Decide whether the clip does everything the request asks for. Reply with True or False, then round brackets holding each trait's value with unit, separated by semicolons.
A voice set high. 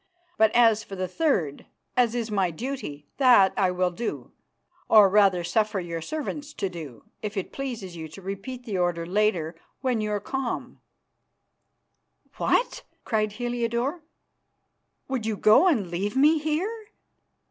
True (215 Hz)